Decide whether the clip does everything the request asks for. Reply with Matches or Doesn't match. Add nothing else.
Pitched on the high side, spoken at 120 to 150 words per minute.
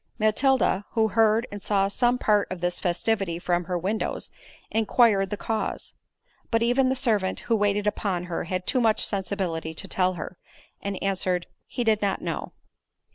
Doesn't match